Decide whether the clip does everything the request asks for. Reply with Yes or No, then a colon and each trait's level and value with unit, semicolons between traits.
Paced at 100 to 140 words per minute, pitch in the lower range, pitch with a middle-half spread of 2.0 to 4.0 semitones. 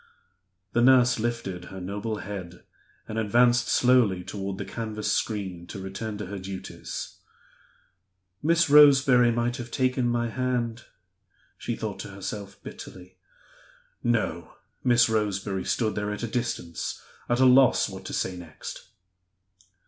Yes: slow, 135 wpm; low, 110 Hz; average, 3.7 semitones